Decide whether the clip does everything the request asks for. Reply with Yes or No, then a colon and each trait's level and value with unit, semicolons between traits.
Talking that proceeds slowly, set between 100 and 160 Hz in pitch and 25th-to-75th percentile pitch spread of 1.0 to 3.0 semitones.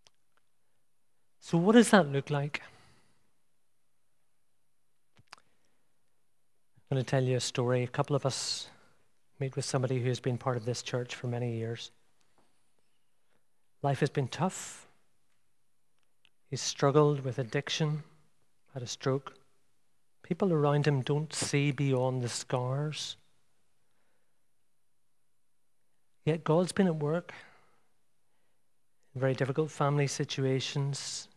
Yes: slow, 110 wpm; medium, 140 Hz; narrow, 2.5 semitones